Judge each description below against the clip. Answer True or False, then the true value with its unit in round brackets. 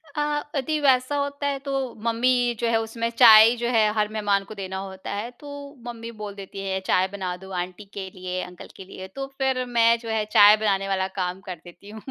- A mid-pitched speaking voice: False (215 Hz)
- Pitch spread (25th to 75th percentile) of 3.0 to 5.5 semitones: True (3.9 semitones)